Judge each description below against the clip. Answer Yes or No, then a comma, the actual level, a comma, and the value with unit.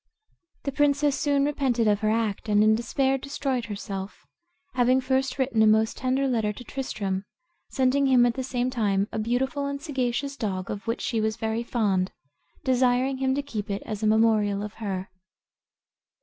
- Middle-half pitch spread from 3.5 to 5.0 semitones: Yes, average, 3.8 semitones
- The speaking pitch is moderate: No, high, 240 Hz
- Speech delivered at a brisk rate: No, average, 175 wpm